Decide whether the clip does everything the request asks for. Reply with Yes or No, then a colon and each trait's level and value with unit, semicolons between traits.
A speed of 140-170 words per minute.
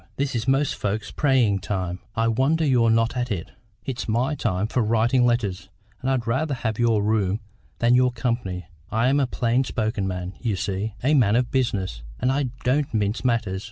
No: average, 190 wpm